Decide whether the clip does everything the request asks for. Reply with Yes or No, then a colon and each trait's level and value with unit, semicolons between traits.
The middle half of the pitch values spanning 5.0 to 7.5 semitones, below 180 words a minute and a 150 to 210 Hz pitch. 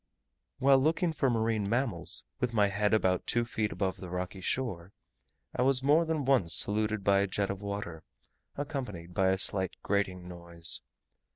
No: average, 5.3 semitones; average, 170 wpm; low, 100 Hz